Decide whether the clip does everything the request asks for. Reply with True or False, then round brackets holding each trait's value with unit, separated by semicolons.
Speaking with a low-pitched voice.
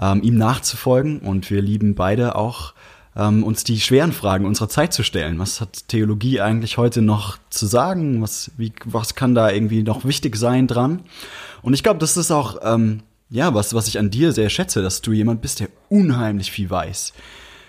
True (110 Hz)